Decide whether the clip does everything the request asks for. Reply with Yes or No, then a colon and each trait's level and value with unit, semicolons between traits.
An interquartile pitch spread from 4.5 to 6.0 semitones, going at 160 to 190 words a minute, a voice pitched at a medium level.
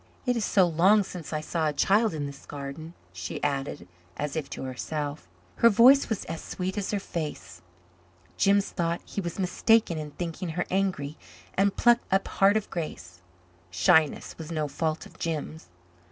Yes: average, 4.8 semitones; average, 175 wpm; medium, 165 Hz